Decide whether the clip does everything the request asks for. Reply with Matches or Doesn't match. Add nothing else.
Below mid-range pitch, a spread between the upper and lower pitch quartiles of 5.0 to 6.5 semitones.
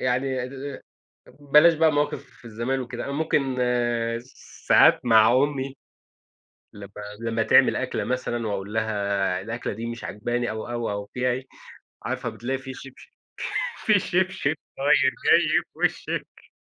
Doesn't match